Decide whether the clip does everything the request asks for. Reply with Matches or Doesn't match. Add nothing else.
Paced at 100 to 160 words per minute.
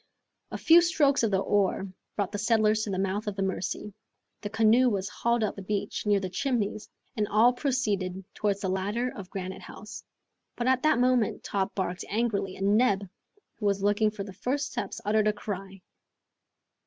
Doesn't match